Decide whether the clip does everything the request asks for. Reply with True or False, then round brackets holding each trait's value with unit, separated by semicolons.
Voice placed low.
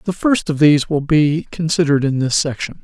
False (150 Hz)